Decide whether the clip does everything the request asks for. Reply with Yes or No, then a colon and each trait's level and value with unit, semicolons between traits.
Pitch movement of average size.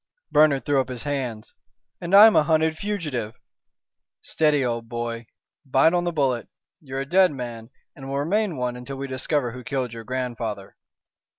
Yes: average, 4.3 semitones